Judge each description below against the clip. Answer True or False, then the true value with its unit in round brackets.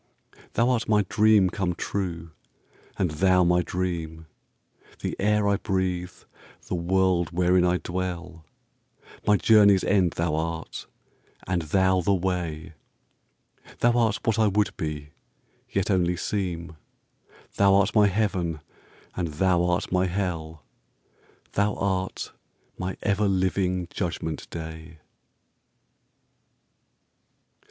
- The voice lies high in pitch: False (90 Hz)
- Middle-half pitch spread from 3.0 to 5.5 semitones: False (2.6 semitones)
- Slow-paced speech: True (105 wpm)